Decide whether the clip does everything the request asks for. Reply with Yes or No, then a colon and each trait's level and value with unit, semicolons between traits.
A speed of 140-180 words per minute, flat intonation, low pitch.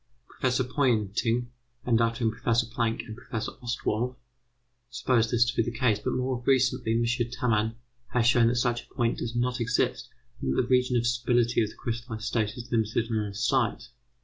No: average, 190 wpm; narrow, 1.5 semitones; low, 120 Hz